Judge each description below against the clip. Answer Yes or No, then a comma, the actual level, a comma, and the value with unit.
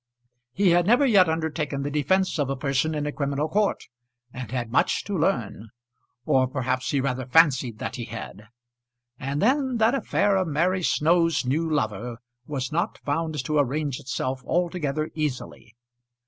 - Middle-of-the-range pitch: Yes, medium, 150 Hz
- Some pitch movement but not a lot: Yes, average, 4.7 semitones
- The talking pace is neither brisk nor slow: Yes, average, 160 wpm